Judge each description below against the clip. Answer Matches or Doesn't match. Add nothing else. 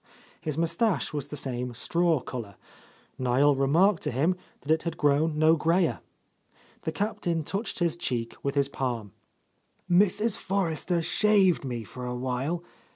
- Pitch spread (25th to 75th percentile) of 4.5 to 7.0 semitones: Matches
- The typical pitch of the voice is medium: Matches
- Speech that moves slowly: Doesn't match